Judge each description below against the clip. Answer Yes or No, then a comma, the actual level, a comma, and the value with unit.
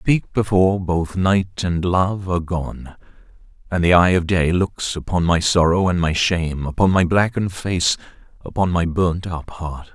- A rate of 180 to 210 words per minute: No, average, 170 wpm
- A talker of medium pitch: No, very low, 90 Hz